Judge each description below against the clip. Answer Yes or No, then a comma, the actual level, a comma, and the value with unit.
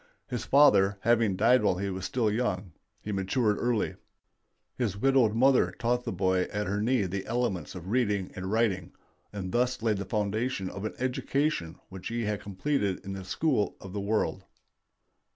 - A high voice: No, low, 105 Hz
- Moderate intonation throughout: Yes, average, 4.1 semitones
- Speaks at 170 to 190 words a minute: Yes, average, 175 wpm